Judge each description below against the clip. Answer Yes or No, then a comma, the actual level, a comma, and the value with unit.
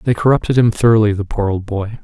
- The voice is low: Yes, low, 110 Hz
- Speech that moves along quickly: Yes, fast, 235 wpm